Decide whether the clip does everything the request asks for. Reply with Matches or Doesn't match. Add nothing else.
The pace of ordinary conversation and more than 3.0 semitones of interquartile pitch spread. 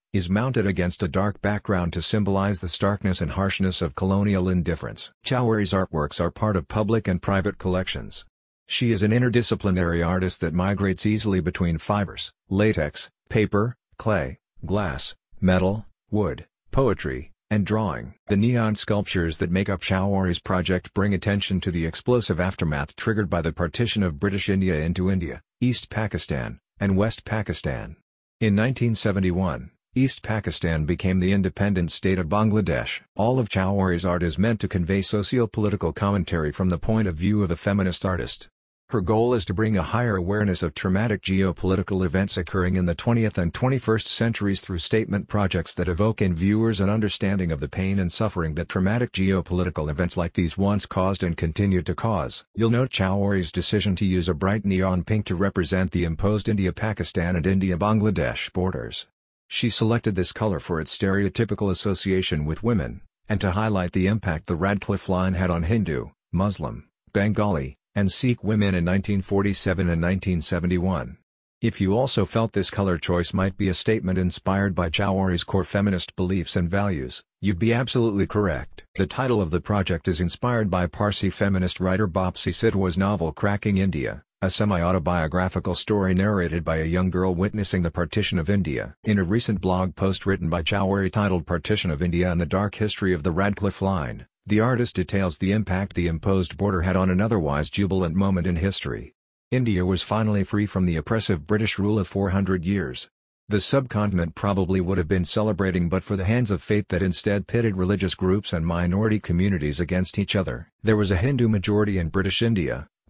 Doesn't match